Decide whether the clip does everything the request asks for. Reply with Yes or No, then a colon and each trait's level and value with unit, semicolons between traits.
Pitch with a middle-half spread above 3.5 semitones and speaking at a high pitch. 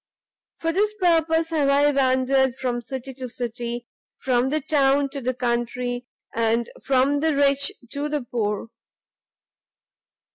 No: average, 2.9 semitones; very high, 265 Hz